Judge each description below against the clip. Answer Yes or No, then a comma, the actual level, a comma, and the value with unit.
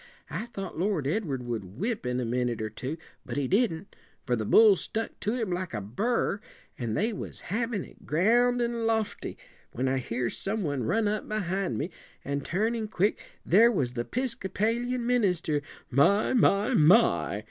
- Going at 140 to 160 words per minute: No, average, 175 wpm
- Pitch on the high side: Yes, high, 195 Hz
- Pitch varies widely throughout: Yes, wide, 8.9 semitones